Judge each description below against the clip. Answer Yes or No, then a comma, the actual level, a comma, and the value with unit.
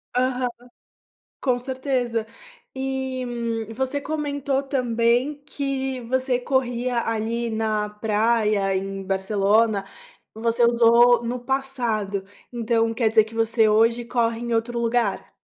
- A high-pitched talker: Yes, high, 235 Hz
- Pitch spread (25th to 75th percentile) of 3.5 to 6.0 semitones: No, narrow, 2.5 semitones